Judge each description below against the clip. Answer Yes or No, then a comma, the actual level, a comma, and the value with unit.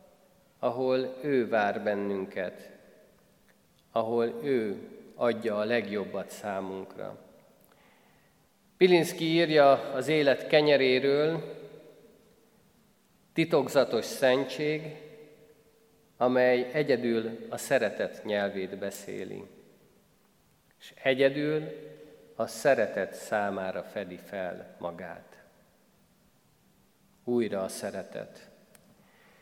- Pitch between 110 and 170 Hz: Yes, low, 130 Hz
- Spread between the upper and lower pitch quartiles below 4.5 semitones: No, average, 5.2 semitones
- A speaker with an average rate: No, slow, 70 wpm